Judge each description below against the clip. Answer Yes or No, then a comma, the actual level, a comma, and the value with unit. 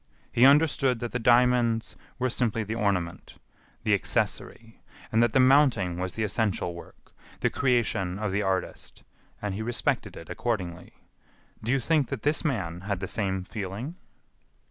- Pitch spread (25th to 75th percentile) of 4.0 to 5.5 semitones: Yes, average, 4.6 semitones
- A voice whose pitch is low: Yes, low, 115 Hz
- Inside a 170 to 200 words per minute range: No, average, 160 wpm